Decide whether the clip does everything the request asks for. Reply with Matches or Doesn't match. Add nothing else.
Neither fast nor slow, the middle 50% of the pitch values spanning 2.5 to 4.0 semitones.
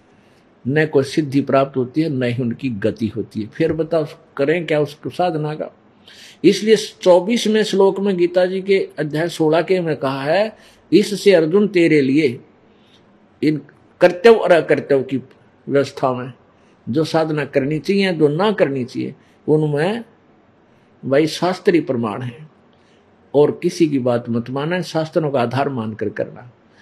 Doesn't match